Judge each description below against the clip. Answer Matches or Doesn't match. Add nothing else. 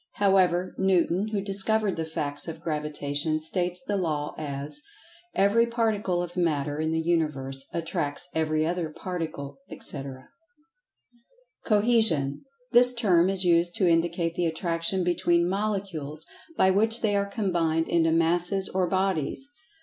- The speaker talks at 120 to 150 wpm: Matches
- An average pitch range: Matches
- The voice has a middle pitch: Matches